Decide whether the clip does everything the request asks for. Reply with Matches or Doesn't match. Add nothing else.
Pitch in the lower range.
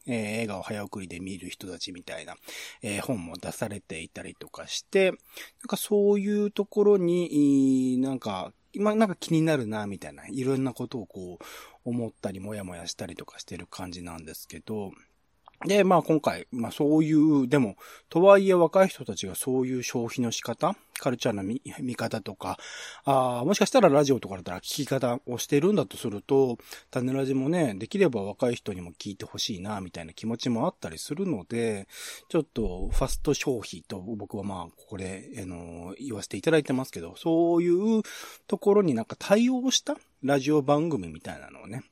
Matches